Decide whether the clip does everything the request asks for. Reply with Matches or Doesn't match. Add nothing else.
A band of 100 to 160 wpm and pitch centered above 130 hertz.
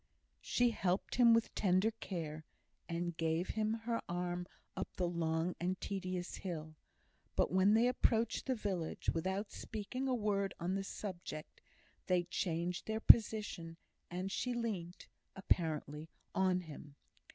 Matches